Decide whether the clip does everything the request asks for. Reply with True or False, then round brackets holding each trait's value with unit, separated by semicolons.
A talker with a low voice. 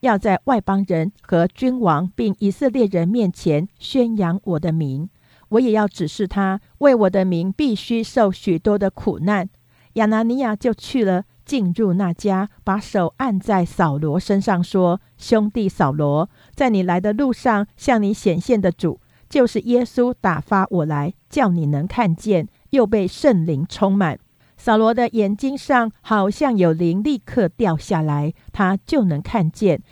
False (195 Hz)